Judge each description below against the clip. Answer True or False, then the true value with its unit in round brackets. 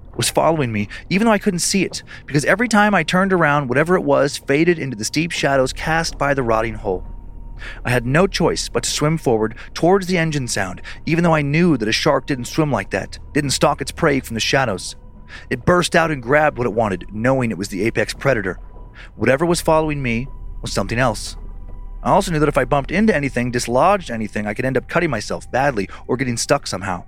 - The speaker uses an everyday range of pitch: False (6.2 semitones)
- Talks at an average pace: False (225 wpm)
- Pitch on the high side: False (135 Hz)